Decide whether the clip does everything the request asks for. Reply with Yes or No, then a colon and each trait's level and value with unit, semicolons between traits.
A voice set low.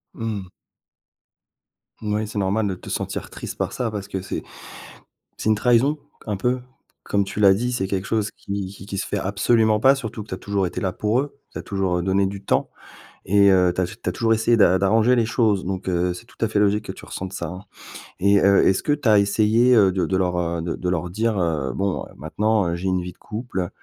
Yes: low, 100 Hz